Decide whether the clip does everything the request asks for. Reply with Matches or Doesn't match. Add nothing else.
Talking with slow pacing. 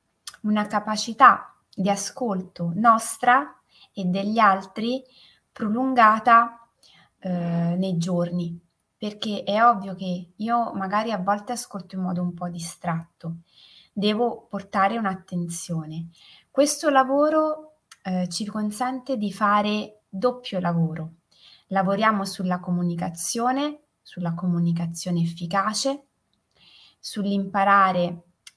Matches